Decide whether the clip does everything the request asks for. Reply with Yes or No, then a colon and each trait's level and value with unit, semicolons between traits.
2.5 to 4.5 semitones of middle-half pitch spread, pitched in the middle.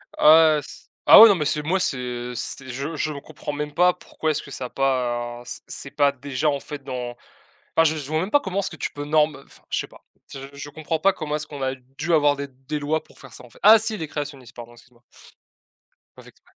Yes: average, 3.1 semitones; medium, 145 Hz